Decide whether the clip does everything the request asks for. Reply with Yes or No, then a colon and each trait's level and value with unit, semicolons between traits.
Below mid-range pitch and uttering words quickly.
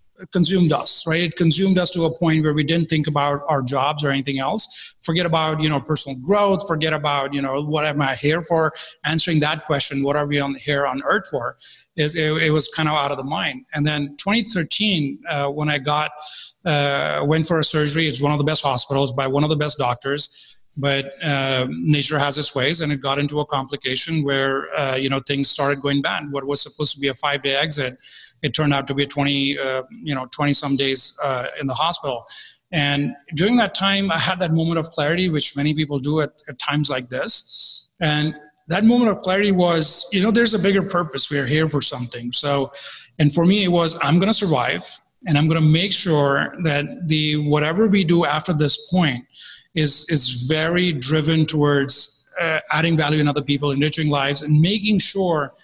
No: medium, 150 Hz; fast, 215 wpm